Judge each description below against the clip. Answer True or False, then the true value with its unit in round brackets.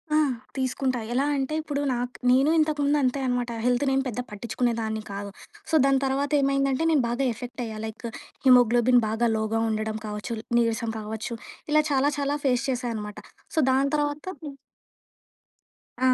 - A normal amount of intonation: True (3.4 semitones)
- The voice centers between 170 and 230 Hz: False (250 Hz)